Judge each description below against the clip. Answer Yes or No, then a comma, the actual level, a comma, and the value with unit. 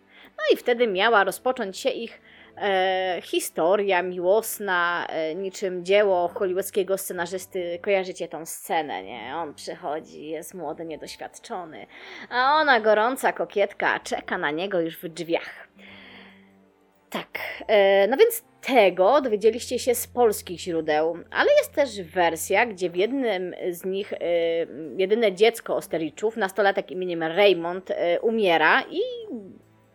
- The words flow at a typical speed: Yes, average, 125 wpm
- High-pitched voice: Yes, high, 195 Hz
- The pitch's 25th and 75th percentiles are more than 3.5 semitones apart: Yes, average, 4.4 semitones